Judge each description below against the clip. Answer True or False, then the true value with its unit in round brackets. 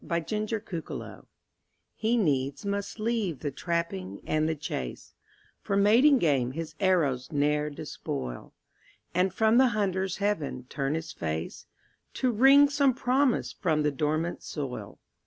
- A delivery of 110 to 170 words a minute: True (140 wpm)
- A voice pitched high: False (170 Hz)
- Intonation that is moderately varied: False (6.7 semitones)